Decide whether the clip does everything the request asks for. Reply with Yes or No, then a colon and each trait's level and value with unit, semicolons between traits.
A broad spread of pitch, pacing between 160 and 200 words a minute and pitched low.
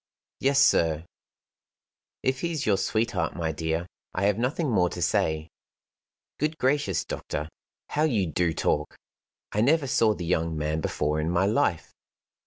No: wide, 8.4 semitones; average, 150 wpm; very low, 95 Hz